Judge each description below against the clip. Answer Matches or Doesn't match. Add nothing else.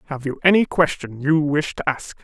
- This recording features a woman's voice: Doesn't match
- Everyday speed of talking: Doesn't match